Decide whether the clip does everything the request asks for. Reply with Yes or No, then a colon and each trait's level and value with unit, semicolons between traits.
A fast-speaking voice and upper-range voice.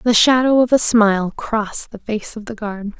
Yes: fast, 220 wpm; high, 225 Hz